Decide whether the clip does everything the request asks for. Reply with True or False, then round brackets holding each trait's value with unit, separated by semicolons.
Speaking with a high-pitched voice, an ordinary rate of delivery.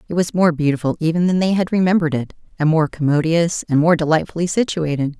False (165 Hz; 195 wpm)